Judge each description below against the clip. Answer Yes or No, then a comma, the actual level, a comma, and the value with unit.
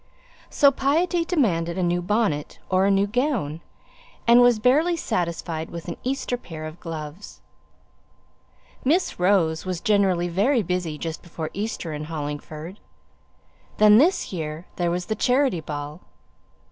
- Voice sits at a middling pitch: Yes, medium, 180 Hz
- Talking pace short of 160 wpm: Yes, average, 140 wpm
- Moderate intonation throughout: No, wide, 6.9 semitones